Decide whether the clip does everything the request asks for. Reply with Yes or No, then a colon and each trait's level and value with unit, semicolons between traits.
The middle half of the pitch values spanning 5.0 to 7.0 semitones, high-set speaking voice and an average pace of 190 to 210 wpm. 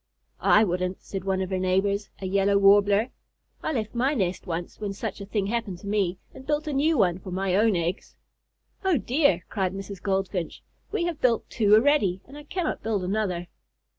No: average, 3.8 semitones; high, 200 Hz; average, 195 wpm